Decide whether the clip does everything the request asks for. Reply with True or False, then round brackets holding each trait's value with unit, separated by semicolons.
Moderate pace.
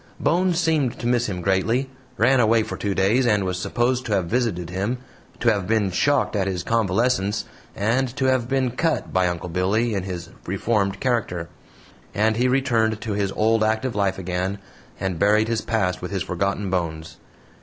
True (185 wpm)